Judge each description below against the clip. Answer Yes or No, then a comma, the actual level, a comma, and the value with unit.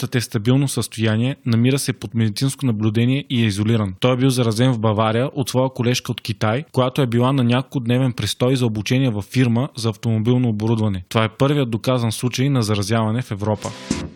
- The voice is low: Yes, low, 120 Hz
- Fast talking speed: Yes, fast, 190 wpm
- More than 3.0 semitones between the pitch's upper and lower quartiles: No, narrow, 2.5 semitones